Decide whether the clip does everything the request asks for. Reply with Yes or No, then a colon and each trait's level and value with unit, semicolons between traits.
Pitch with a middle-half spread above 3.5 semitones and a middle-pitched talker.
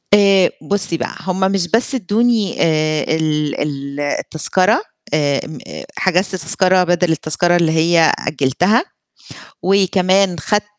Yes: average, 4.0 semitones; medium, 180 Hz